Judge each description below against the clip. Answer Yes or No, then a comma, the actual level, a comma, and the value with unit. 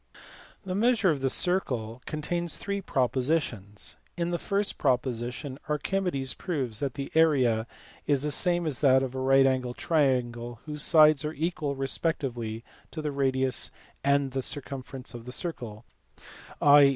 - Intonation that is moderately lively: Yes, average, 3.9 semitones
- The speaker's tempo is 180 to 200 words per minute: No, average, 155 wpm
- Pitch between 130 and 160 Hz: Yes, low, 135 Hz